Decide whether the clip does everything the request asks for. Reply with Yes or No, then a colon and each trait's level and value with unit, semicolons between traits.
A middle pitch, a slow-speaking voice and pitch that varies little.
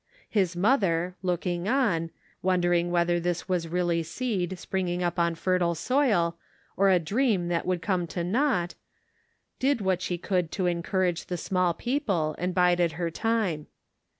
No: medium, 180 Hz; average, 160 wpm; narrow, 2.0 semitones